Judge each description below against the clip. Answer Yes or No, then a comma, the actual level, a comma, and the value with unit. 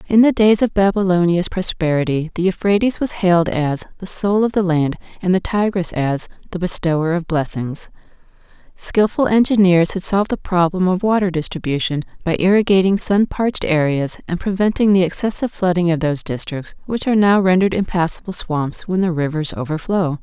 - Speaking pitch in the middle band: Yes, medium, 180 Hz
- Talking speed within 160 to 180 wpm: Yes, average, 165 wpm